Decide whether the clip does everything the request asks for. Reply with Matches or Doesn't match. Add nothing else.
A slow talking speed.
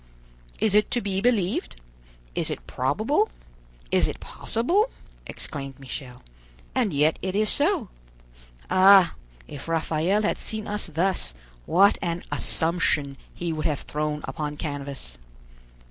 Matches